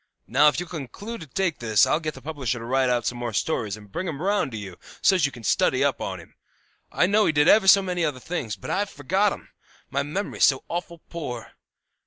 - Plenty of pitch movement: Yes, wide, 6.4 semitones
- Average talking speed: No, fast, 240 wpm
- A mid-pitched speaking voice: Yes, medium, 150 Hz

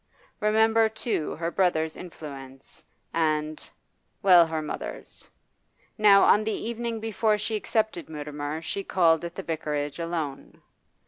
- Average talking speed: No, slow, 125 wpm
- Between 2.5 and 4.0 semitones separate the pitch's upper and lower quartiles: No, wide, 5.5 semitones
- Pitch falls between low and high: Yes, medium, 170 Hz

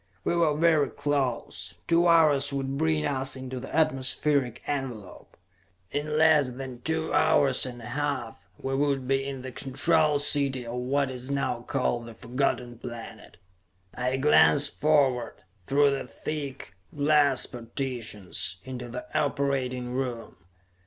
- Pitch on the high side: No, low, 135 Hz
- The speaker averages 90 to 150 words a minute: Yes, average, 140 wpm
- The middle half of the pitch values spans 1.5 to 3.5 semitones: Yes, average, 2.7 semitones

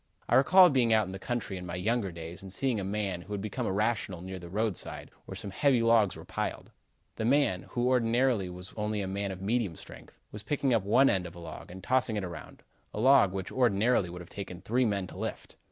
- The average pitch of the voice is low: Yes, low, 105 Hz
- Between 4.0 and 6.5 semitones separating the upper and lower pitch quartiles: Yes, average, 4.3 semitones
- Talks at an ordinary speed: No, fast, 235 wpm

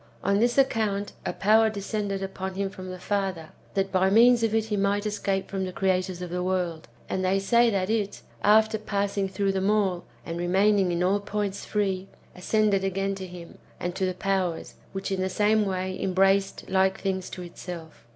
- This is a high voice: Yes, high, 195 Hz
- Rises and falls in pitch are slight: Yes, narrow, 1.7 semitones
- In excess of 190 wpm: Yes, average, 200 wpm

